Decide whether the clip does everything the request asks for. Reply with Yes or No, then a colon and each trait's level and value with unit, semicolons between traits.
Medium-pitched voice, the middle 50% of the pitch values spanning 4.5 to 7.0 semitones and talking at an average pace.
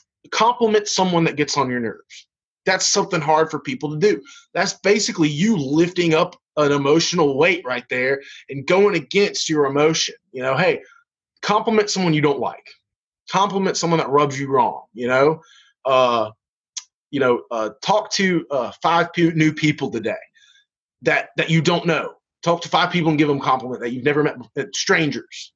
Yes: medium, 160 Hz; average, 5.0 semitones; average, 175 wpm